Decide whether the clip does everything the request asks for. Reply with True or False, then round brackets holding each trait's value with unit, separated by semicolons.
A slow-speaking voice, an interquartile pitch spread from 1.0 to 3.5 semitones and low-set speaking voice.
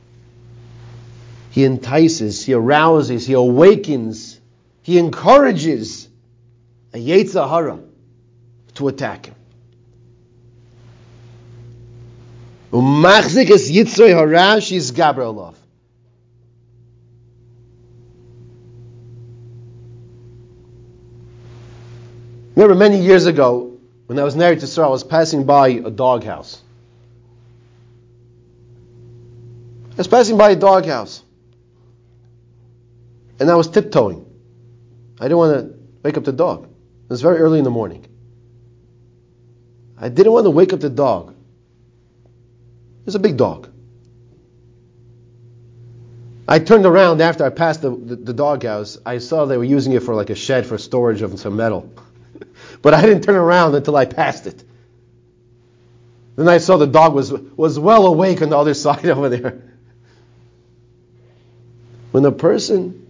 True (115 wpm; 3.2 semitones; 120 Hz)